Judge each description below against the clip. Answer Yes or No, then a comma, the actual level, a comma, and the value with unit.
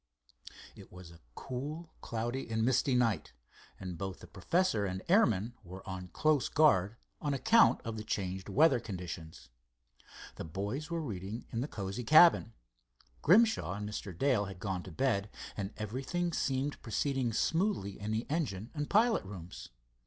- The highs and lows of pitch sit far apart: Yes, wide, 7.3 semitones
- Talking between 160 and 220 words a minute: No, average, 150 wpm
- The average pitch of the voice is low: Yes, low, 115 Hz